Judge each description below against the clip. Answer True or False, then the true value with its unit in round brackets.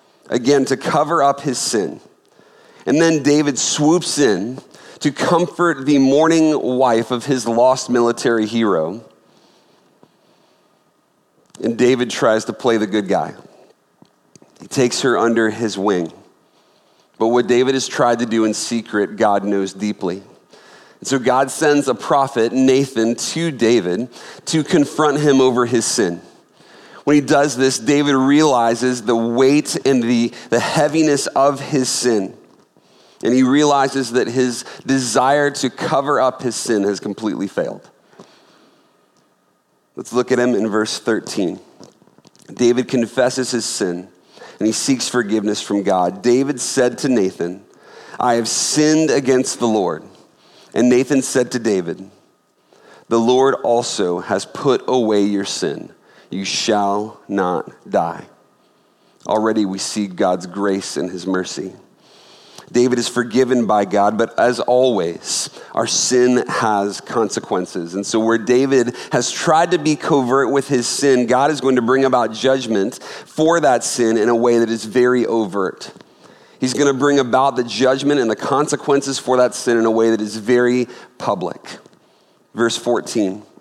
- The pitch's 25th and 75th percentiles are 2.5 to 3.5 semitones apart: True (3.2 semitones)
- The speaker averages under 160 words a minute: True (150 wpm)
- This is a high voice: False (125 Hz)